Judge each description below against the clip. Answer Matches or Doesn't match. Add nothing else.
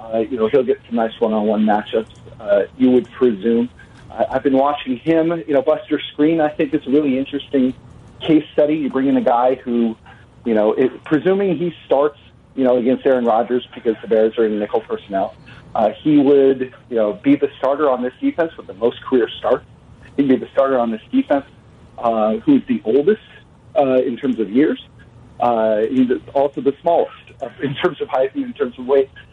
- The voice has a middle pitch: Doesn't match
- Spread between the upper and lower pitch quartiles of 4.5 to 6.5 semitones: Doesn't match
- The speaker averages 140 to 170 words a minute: Doesn't match